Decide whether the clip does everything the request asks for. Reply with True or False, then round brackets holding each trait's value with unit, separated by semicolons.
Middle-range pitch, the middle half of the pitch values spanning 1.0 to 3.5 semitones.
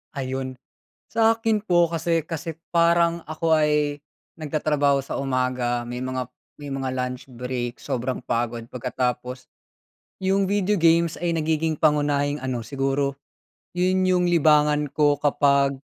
False (145 Hz; 4.4 semitones)